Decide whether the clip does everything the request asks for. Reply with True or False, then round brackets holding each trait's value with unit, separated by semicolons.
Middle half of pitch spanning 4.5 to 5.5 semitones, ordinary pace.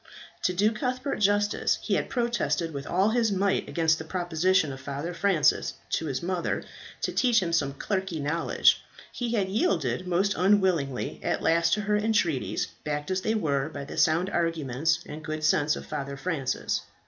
True (4.9 semitones; 175 wpm)